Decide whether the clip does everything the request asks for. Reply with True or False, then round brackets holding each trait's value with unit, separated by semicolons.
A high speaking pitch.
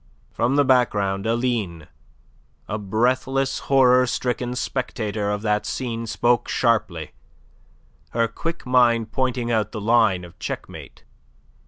False (115 Hz)